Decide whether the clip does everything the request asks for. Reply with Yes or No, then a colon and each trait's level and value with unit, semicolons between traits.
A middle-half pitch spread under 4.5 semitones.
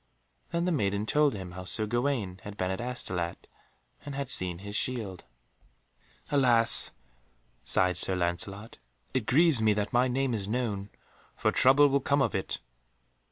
No: wide, 5.5 semitones